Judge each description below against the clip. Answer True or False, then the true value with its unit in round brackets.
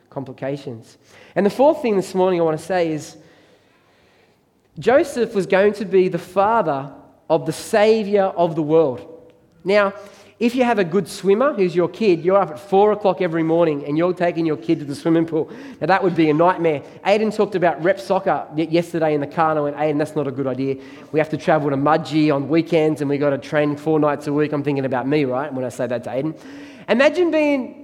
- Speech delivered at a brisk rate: True (225 wpm)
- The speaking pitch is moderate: True (165 Hz)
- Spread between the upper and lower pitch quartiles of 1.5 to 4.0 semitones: False (4.7 semitones)